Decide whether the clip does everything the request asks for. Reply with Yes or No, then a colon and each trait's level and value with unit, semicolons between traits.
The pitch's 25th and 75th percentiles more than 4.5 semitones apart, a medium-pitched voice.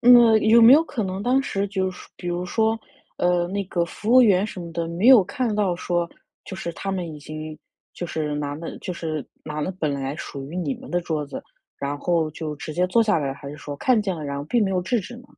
Yes: average, 5.3 semitones; medium, 175 Hz